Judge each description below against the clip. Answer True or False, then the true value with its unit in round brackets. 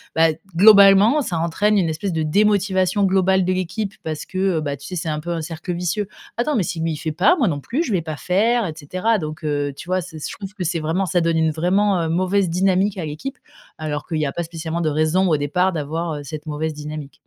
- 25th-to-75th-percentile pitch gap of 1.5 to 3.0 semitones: False (3.6 semitones)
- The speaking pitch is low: False (170 Hz)